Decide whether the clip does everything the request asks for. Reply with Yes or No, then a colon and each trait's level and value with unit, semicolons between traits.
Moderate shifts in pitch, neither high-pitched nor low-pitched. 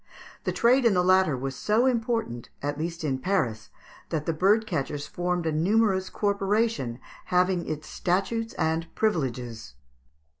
No: wide, 6.2 semitones; medium, 180 Hz